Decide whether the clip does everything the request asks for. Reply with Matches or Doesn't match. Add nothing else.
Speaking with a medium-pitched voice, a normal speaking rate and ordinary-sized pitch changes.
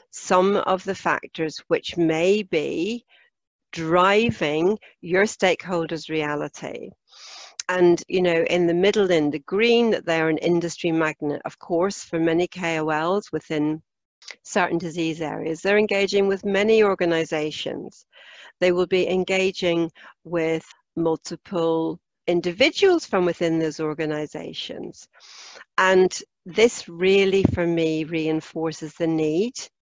Doesn't match